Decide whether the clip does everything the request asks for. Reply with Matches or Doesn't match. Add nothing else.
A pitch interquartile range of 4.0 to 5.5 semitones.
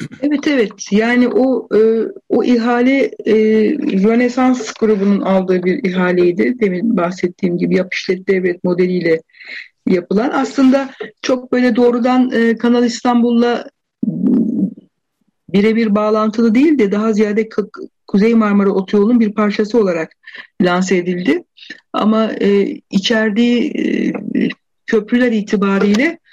Doesn't match